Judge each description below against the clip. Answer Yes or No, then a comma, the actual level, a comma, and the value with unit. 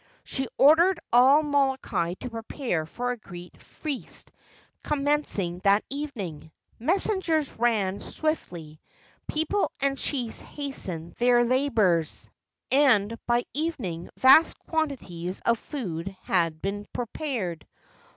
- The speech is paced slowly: Yes, slow, 100 wpm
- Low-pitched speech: No, high, 240 Hz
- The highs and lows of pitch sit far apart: Yes, wide, 7.5 semitones